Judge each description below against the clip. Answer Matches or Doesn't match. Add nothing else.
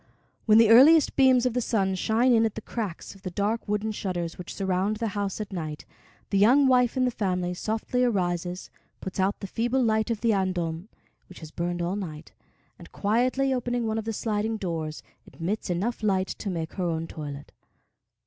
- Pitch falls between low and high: Doesn't match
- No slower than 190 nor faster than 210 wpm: Matches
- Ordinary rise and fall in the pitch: Matches